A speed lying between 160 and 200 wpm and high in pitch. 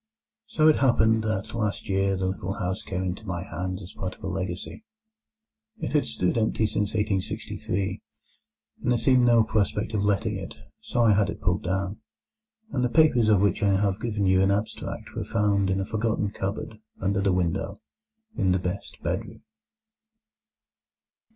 No: average, 175 wpm; low, 100 Hz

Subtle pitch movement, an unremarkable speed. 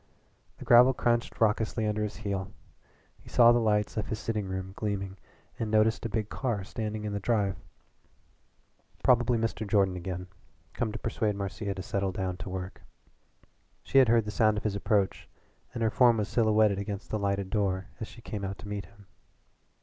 Yes: narrow, 2.3 semitones; average, 190 wpm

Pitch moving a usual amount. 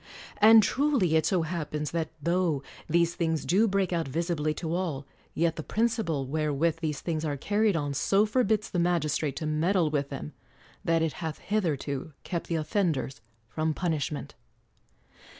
Yes: average, 3.2 semitones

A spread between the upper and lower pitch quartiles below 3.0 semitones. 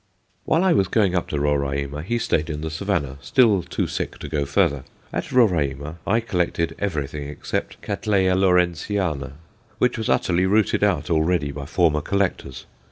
No: average, 5.2 semitones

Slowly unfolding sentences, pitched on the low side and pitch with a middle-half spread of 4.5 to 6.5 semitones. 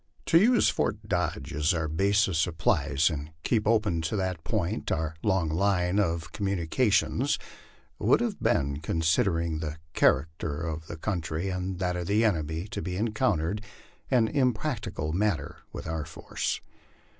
No: average, 150 wpm; very low, 90 Hz; average, 4.8 semitones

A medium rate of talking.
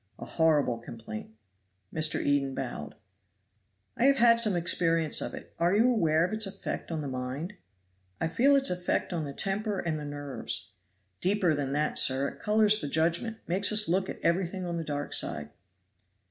Yes: average, 180 wpm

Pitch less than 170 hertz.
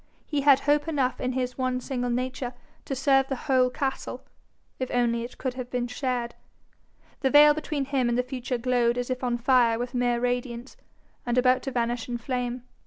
No: very high, 250 Hz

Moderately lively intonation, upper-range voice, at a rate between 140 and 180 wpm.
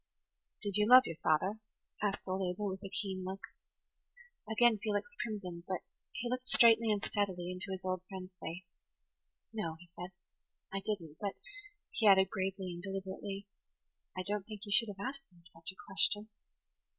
No: narrow, 2.3 semitones; high, 195 Hz; average, 170 wpm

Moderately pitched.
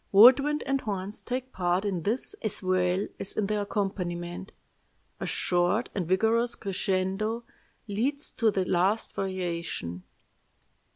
No: high, 195 Hz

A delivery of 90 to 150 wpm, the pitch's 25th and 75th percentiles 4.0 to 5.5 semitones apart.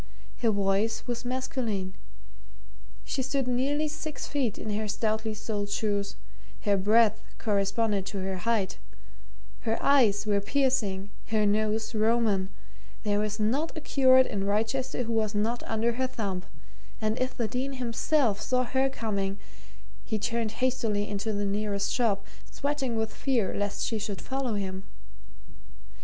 No: average, 145 wpm; average, 3.5 semitones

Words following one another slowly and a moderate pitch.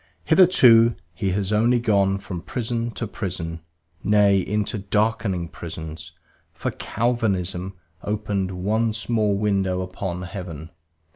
No: slow, 115 wpm; low, 100 Hz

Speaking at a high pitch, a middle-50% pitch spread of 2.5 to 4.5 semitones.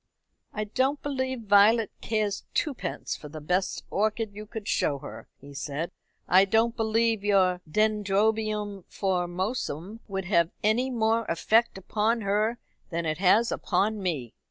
Yes: high, 210 Hz; average, 3.4 semitones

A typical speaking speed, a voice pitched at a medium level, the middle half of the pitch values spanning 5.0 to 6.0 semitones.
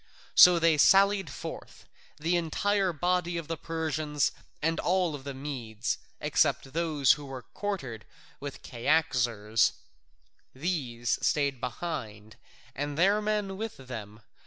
No: slow, 120 wpm; medium, 150 Hz; average, 5.3 semitones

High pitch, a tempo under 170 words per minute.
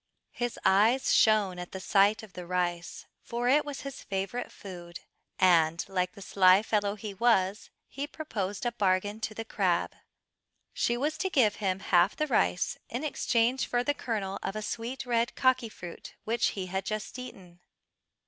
No: high, 210 Hz; average, 175 wpm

